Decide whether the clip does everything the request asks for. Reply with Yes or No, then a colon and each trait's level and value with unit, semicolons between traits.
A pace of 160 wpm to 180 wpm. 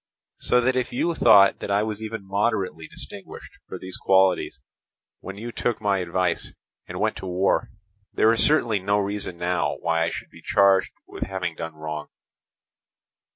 Yes: average, 170 wpm